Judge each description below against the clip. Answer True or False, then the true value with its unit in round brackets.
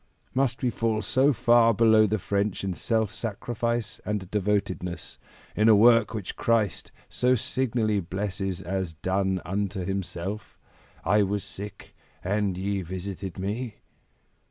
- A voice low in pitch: True (105 Hz)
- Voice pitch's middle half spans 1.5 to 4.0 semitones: True (2.9 semitones)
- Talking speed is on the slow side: True (130 wpm)